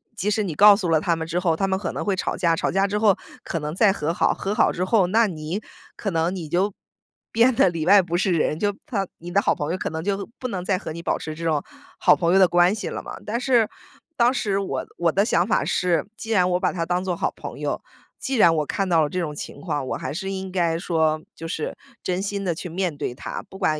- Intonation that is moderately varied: Yes, average, 3.3 semitones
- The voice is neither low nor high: Yes, medium, 180 Hz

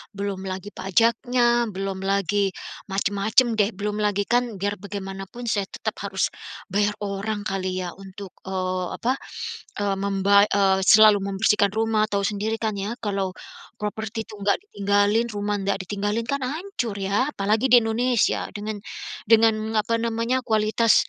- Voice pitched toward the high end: Yes, high, 205 Hz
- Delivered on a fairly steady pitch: Yes, narrow, 2.2 semitones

